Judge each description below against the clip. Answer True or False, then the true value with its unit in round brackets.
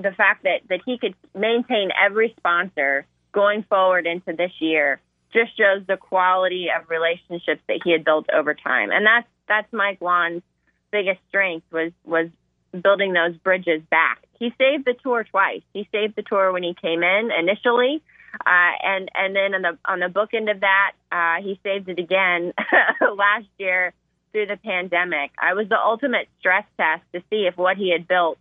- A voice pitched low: False (190 Hz)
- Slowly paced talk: False (185 wpm)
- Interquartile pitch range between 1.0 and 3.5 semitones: True (3.0 semitones)